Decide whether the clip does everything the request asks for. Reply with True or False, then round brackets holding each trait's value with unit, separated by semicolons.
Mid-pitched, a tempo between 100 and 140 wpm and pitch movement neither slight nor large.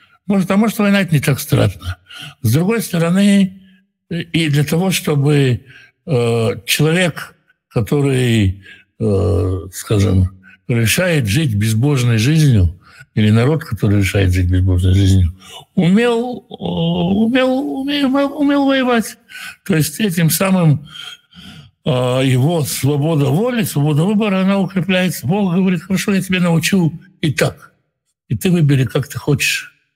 False (155 Hz; 130 wpm; 8.0 semitones)